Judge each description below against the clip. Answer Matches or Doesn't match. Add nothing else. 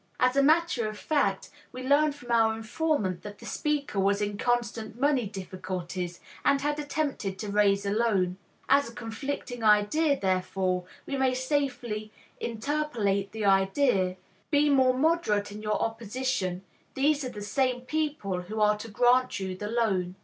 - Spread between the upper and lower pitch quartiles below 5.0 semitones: Doesn't match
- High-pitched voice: Matches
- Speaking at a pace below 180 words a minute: Matches